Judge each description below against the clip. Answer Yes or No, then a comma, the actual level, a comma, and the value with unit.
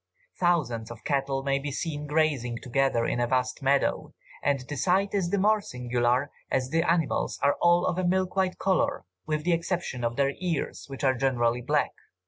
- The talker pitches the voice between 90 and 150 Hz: Yes, medium, 140 Hz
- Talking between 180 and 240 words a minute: Yes, average, 190 wpm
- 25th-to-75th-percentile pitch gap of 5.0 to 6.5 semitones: Yes, average, 5.3 semitones